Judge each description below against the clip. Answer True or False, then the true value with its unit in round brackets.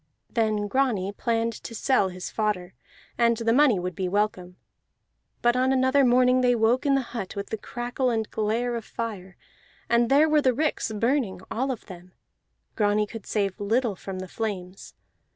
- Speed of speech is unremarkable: True (175 wpm)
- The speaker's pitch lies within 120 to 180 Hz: False (225 Hz)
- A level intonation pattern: False (3.9 semitones)